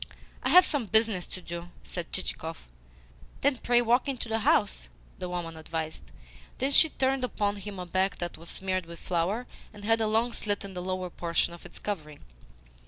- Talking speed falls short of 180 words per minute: No, average, 190 wpm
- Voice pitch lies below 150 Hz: No, high, 195 Hz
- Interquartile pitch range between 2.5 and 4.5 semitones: No, average, 4.9 semitones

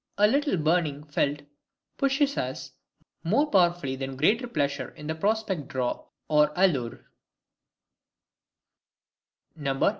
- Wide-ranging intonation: Yes, wide, 6.8 semitones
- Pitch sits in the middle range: Yes, medium, 155 Hz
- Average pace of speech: No, slow, 95 wpm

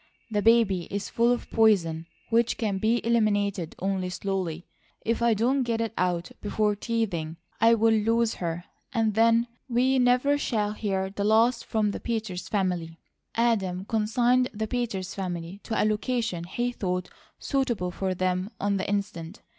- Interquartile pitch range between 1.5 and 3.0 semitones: No, average, 3.9 semitones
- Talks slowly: No, average, 155 wpm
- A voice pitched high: Yes, high, 210 Hz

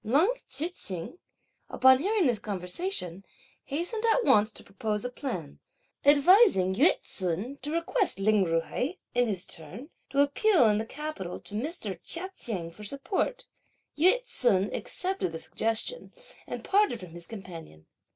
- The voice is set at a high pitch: Yes, high, 245 Hz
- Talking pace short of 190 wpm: Yes, average, 150 wpm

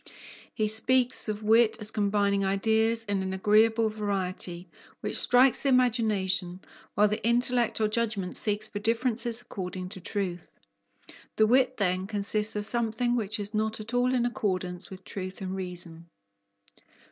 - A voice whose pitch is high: Yes, high, 210 Hz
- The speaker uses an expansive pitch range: No, average, 3.1 semitones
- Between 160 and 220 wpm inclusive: No, average, 150 wpm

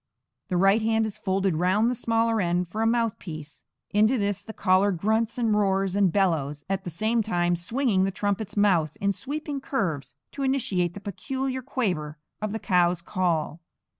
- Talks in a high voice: Yes, high, 200 Hz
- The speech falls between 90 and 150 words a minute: No, average, 175 wpm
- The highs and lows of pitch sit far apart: No, average, 4.1 semitones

